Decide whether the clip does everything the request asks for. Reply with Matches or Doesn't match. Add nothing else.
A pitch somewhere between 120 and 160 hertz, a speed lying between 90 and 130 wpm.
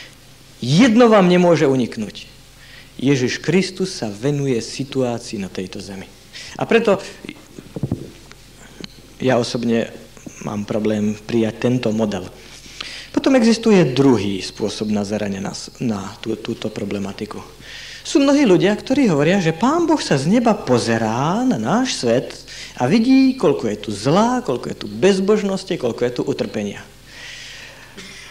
Matches